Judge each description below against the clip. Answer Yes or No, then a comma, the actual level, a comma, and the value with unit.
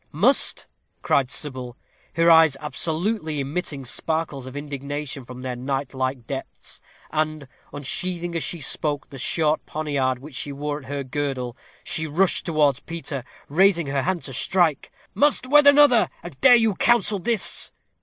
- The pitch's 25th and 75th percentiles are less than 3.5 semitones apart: No, average, 4.1 semitones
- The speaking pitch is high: No, medium, 150 Hz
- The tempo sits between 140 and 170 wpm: Yes, average, 155 wpm